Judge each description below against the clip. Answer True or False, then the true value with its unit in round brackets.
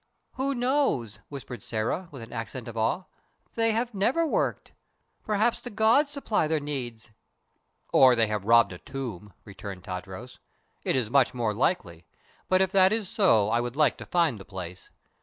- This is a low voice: True (130 Hz)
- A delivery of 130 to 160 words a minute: False (175 wpm)